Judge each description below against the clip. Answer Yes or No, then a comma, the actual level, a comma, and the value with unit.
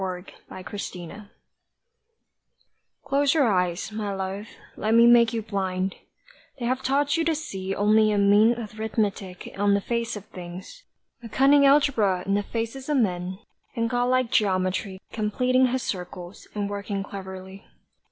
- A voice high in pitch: Yes, high, 210 Hz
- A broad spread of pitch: No, average, 4.1 semitones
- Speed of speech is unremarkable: Yes, average, 150 wpm